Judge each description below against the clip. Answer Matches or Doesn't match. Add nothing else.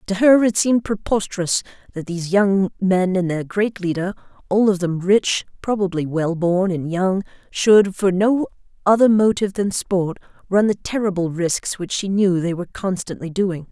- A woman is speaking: Matches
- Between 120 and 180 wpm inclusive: Matches